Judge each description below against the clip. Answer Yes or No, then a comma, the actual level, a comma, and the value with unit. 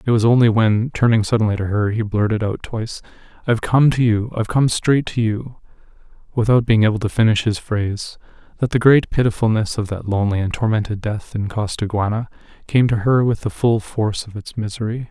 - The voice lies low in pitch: Yes, low, 110 Hz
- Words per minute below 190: No, average, 195 wpm